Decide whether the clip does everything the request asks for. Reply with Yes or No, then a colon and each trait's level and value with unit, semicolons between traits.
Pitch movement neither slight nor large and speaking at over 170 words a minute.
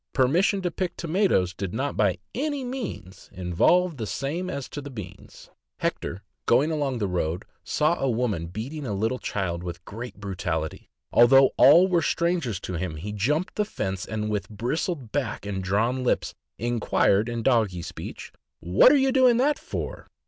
No: wide, 8.8 semitones; average, 180 wpm